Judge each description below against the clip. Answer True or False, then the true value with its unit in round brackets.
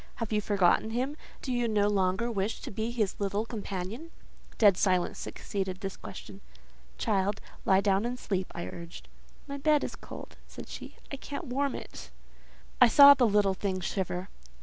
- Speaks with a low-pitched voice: False (210 Hz)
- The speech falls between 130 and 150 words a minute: False (170 wpm)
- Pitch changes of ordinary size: True (4.1 semitones)